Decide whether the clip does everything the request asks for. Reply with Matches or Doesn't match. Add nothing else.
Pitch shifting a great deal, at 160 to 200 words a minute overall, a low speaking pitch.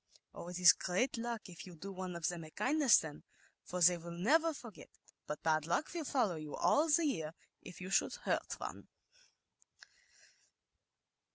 Doesn't match